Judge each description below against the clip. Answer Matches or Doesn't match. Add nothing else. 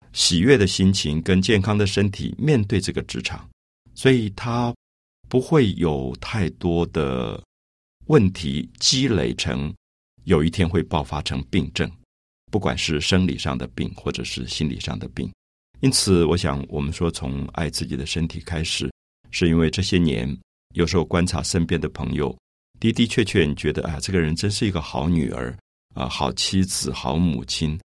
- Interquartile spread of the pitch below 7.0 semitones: Matches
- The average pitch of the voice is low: Matches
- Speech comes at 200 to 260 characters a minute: Matches